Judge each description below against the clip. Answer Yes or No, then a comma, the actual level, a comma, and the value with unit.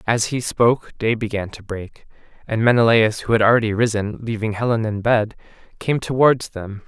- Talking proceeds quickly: No, average, 175 wpm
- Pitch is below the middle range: Yes, low, 110 Hz